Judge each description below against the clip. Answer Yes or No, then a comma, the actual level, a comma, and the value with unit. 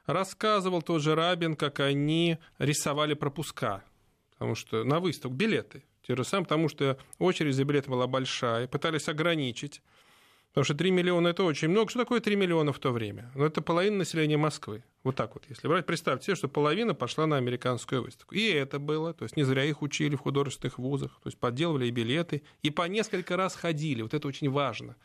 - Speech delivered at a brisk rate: Yes, fast, 200 wpm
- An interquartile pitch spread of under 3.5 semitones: No, average, 4.2 semitones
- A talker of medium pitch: Yes, medium, 150 Hz